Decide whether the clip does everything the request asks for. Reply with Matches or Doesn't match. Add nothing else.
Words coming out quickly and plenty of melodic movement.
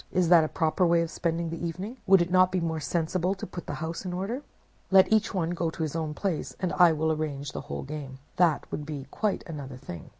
Doesn't match